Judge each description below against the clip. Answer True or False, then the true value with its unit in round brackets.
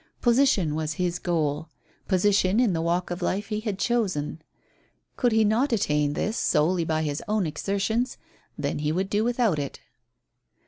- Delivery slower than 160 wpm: False (165 wpm)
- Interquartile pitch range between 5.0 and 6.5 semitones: True (5.4 semitones)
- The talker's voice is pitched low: False (185 Hz)